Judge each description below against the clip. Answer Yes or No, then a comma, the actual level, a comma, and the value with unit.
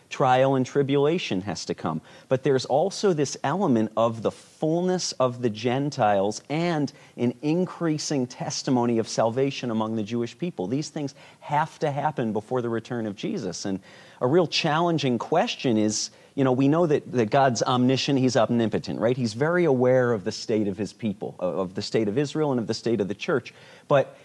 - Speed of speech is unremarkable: Yes, average, 190 wpm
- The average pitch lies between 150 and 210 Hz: No, low, 130 Hz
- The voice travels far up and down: No, average, 4.7 semitones